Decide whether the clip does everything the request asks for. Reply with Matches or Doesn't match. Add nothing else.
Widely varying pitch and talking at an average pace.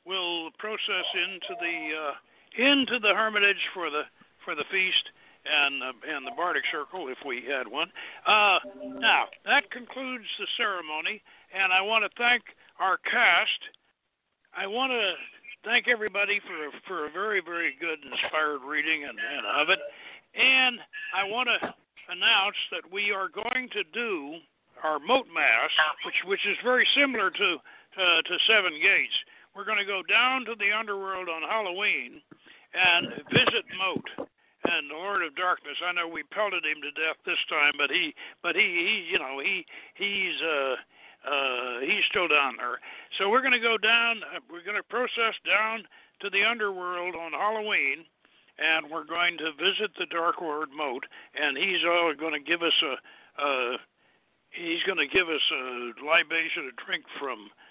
Matches